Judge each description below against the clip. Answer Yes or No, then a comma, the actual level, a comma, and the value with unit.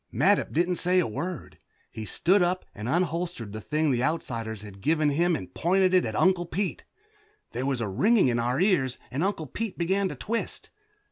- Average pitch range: No, wide, 7.0 semitones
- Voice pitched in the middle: Yes, medium, 165 Hz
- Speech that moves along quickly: No, average, 195 wpm